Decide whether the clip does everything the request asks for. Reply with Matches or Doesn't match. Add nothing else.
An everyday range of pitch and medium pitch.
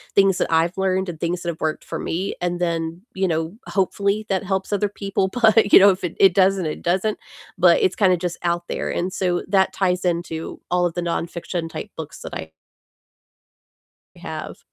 Doesn't match